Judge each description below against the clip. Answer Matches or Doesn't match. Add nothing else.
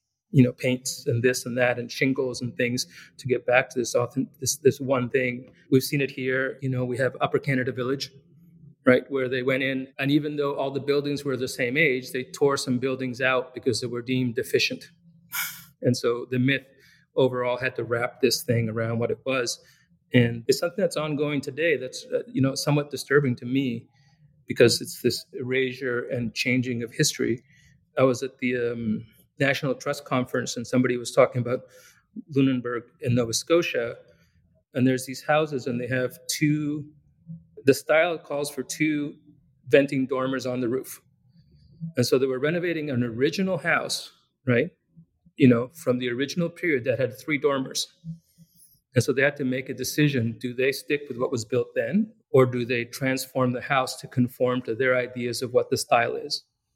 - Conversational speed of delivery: Matches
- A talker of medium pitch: Doesn't match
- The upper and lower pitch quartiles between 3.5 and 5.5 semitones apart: Doesn't match